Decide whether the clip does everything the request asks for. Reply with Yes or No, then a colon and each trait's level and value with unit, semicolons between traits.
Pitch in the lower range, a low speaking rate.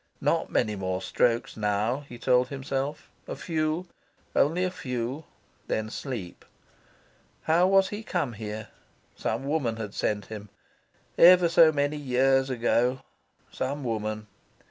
Yes: low, 130 Hz; slow, 130 wpm